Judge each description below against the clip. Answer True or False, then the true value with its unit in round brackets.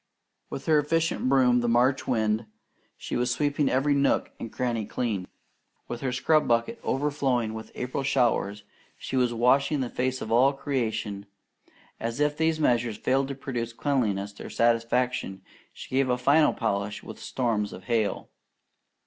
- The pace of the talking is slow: False (160 wpm)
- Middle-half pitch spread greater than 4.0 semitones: False (3.1 semitones)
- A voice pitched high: False (125 Hz)